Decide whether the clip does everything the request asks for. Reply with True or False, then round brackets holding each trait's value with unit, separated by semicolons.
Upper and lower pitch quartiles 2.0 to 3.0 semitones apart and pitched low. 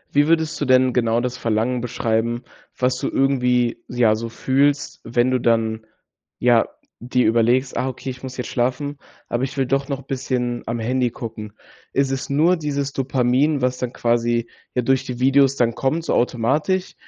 True (2.4 semitones; 125 Hz)